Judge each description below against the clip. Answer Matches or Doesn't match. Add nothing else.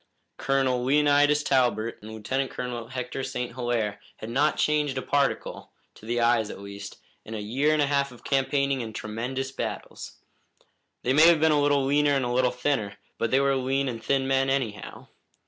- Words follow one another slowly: Doesn't match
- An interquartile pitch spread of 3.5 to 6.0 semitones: Doesn't match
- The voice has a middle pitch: Doesn't match